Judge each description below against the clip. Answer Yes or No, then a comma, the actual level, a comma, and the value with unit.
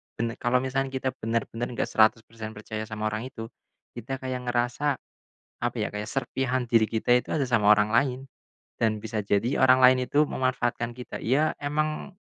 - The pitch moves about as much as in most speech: Yes, average, 3.0 semitones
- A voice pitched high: No, low, 120 Hz